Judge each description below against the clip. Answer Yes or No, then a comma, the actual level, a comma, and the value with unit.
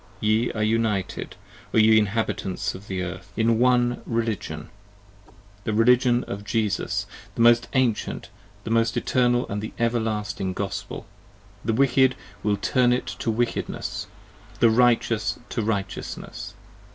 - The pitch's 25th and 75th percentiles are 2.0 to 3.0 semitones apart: Yes, narrow, 2.6 semitones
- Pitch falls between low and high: No, low, 115 Hz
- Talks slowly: Yes, slow, 125 wpm